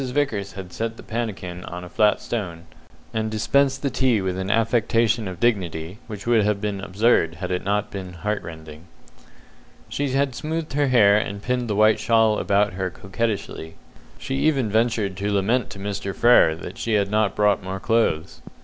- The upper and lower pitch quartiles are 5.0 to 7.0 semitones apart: No, average, 3.5 semitones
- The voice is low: Yes, low, 105 Hz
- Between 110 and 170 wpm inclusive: No, average, 185 wpm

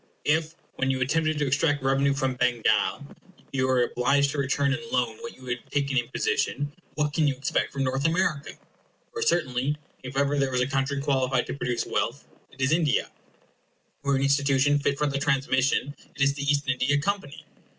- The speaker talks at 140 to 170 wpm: No, average, 190 wpm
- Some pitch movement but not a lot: No, narrow, 1.8 semitones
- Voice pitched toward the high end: No, medium, 140 Hz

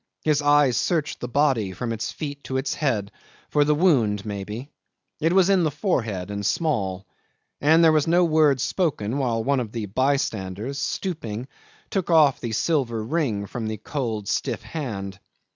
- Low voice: Yes, low, 130 Hz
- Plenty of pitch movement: Yes, wide, 6.1 semitones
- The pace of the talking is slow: No, average, 175 wpm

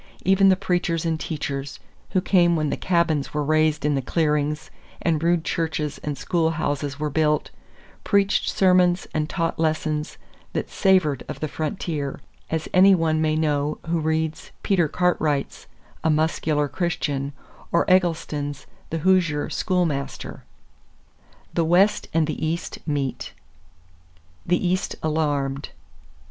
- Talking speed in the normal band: No, slow, 130 wpm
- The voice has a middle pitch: Yes, medium, 160 Hz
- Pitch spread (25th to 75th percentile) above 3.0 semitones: No, average, 2.7 semitones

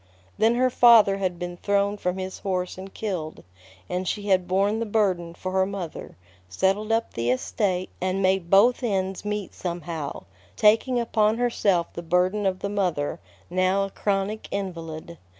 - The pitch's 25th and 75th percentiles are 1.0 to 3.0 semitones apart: Yes, narrow, 2.6 semitones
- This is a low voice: No, high, 190 Hz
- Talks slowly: No, average, 165 wpm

